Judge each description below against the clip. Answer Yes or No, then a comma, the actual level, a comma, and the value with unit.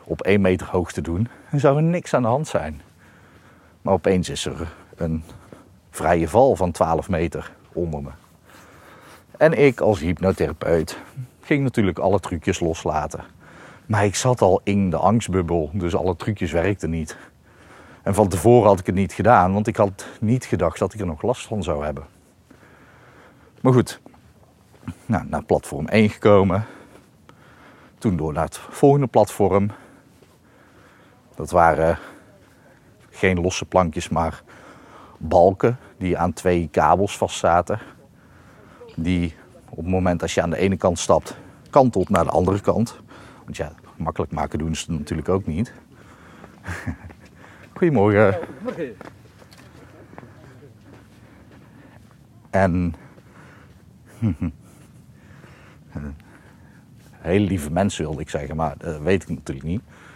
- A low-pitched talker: Yes, very low, 95 Hz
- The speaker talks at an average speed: No, slow, 130 wpm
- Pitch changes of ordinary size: Yes, average, 4.2 semitones